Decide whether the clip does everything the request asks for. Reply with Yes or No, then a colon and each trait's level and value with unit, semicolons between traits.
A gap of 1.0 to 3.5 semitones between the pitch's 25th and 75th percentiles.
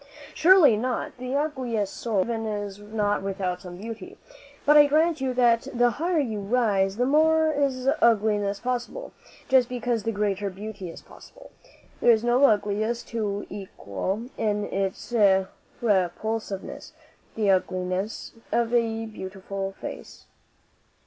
No: average, 3.9 semitones